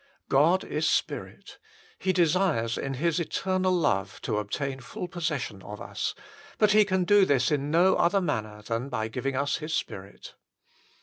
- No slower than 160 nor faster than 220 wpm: Yes, average, 165 wpm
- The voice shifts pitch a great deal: Yes, wide, 6.7 semitones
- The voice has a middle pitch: Yes, medium, 150 Hz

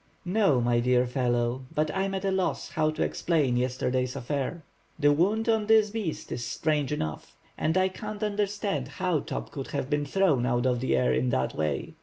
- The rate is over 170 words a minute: Yes, average, 200 wpm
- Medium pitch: Yes, medium, 145 Hz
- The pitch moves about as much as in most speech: No, wide, 7.4 semitones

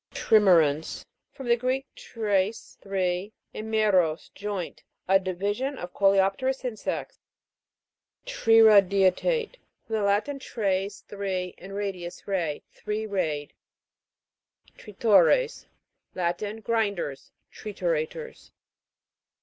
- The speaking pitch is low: No, high, 200 Hz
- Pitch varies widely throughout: No, average, 3.3 semitones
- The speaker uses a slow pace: Yes, slow, 95 wpm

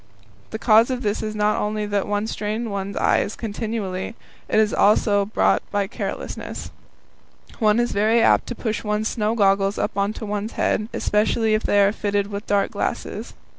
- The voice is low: No, high, 210 Hz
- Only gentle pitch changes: Yes, narrow, 1.3 semitones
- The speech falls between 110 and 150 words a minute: No, average, 185 wpm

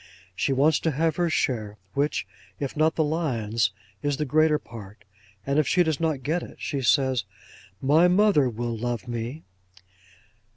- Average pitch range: Yes, average, 4.8 semitones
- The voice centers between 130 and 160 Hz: Yes, medium, 140 Hz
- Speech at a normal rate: Yes, average, 165 wpm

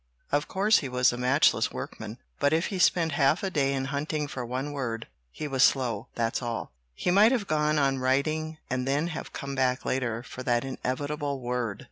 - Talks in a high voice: No, low, 135 Hz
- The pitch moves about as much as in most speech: Yes, average, 3.3 semitones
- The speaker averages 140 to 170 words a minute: No, average, 200 wpm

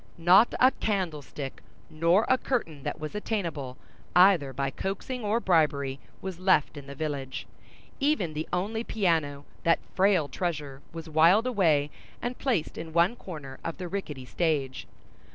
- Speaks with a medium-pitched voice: Yes, medium, 165 Hz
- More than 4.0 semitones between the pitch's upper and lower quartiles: Yes, average, 5.2 semitones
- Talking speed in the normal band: Yes, average, 150 wpm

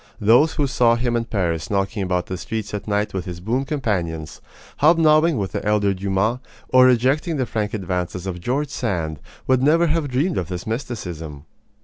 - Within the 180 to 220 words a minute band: Yes, average, 185 wpm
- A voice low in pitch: Yes, low, 110 Hz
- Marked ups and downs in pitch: Yes, wide, 6.0 semitones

